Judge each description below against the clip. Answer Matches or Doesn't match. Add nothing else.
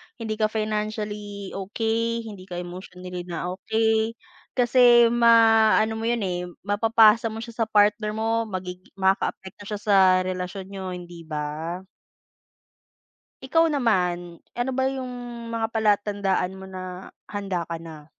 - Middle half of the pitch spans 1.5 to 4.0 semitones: Matches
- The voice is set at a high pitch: Matches